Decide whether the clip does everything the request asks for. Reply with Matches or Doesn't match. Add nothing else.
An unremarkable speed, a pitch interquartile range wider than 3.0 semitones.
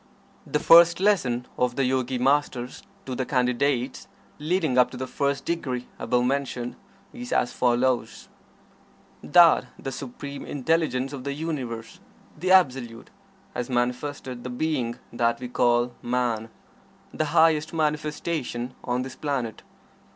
Doesn't match